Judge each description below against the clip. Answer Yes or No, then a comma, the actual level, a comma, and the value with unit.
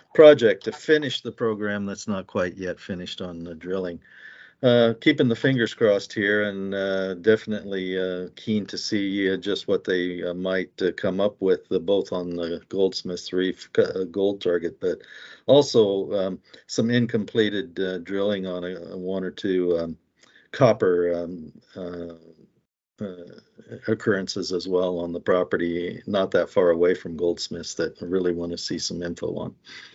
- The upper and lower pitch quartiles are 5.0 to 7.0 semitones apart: No, average, 3.0 semitones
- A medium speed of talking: Yes, average, 170 wpm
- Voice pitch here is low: Yes, very low, 95 Hz